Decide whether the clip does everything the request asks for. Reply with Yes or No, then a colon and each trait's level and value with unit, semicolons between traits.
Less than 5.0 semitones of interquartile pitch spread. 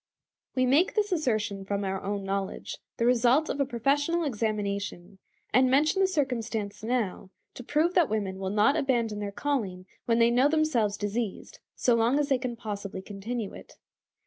No: wide, 5.4 semitones